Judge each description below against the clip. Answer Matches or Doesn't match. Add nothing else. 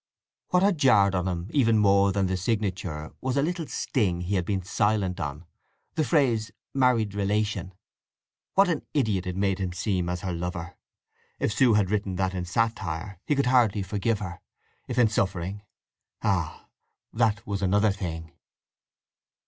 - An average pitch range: Matches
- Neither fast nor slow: Matches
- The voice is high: Doesn't match